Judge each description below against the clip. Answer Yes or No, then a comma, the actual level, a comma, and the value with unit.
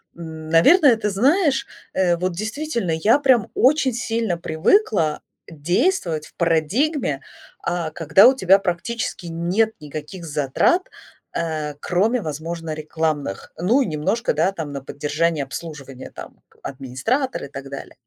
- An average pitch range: No, wide, 6.8 semitones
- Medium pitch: Yes, medium, 170 Hz